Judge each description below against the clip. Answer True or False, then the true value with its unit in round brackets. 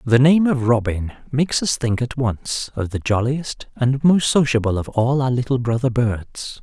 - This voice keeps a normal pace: True (190 wpm)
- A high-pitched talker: False (125 Hz)